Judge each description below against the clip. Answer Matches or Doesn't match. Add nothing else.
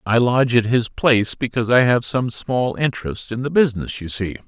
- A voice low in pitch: Matches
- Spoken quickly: Matches